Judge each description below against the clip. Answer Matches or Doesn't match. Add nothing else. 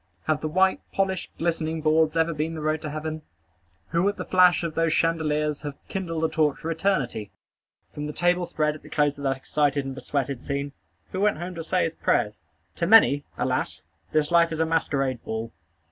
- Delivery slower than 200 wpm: Doesn't match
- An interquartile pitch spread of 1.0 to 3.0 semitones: Matches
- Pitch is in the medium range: Matches